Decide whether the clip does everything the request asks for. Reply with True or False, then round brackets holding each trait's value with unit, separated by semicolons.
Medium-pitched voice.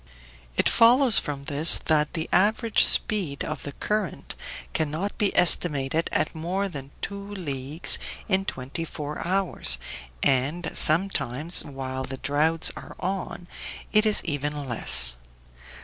True (160 Hz)